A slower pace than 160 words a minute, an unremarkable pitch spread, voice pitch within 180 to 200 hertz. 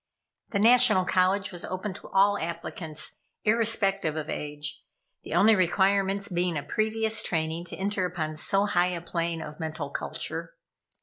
Yes: average, 150 wpm; average, 3.7 semitones; medium, 185 Hz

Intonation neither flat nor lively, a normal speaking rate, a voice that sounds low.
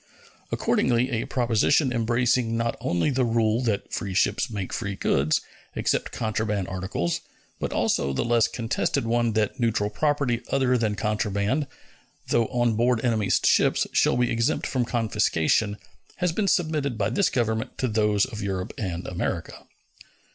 Yes: average, 3.0 semitones; average, 150 wpm; low, 115 Hz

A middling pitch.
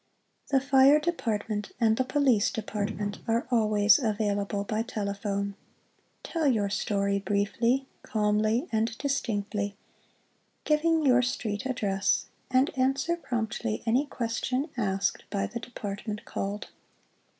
No: high, 220 Hz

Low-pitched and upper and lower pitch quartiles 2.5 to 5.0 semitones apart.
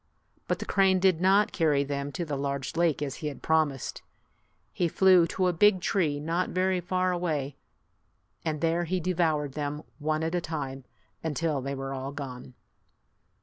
No: medium, 160 Hz; average, 4.0 semitones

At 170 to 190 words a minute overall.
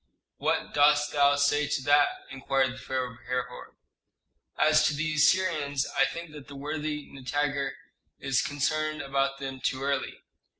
No: average, 155 wpm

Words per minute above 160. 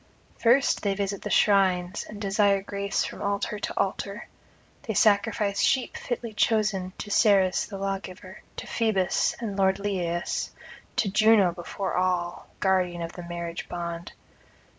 No: average, 145 wpm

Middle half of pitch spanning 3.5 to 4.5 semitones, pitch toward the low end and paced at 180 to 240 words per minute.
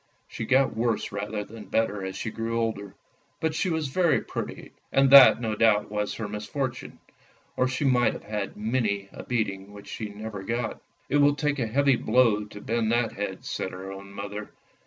Yes: average, 3.8 semitones; low, 110 Hz; average, 200 wpm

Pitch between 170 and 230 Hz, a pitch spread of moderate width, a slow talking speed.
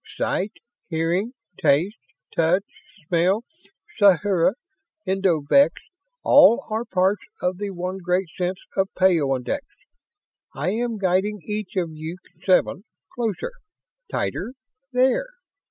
Yes: high, 190 Hz; average, 3.3 semitones; slow, 105 wpm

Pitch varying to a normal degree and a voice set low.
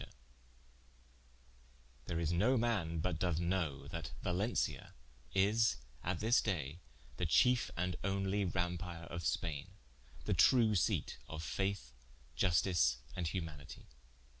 Yes: average, 3.2 semitones; very low, 90 Hz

